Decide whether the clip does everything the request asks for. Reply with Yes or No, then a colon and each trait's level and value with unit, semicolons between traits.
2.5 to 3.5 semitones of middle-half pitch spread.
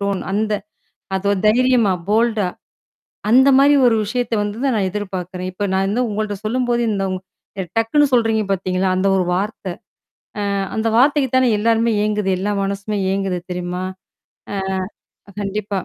Yes: average, 3.1 semitones